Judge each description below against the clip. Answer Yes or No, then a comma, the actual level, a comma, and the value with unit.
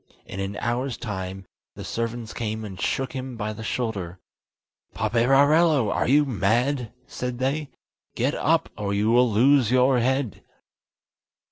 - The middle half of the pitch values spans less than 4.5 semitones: Yes, average, 3.8 semitones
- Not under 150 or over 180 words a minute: No, average, 140 wpm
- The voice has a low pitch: Yes, low, 120 Hz